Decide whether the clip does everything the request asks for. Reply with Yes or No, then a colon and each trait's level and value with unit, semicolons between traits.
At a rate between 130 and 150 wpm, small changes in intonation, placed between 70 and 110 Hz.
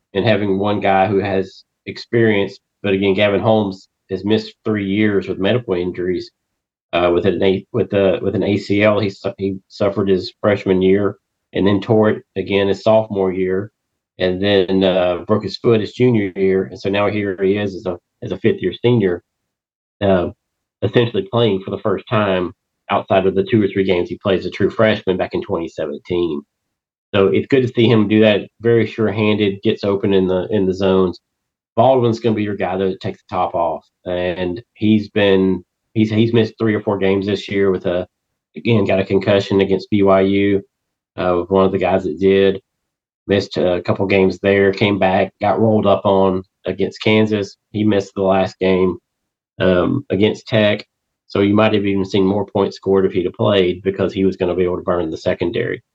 No: average, 200 wpm; narrow, 1.9 semitones; low, 100 Hz